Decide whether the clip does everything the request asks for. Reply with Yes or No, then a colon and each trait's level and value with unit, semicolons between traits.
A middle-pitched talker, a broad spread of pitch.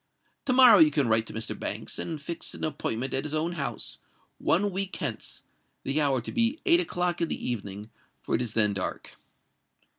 Yes: medium, 155 Hz; wide, 7.6 semitones